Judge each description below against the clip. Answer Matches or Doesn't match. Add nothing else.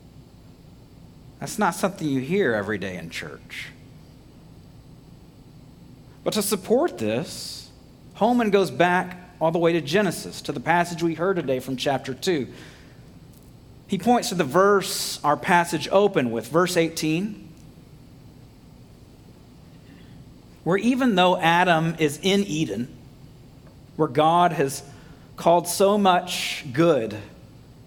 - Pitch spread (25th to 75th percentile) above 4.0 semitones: Matches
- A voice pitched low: Doesn't match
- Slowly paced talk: Matches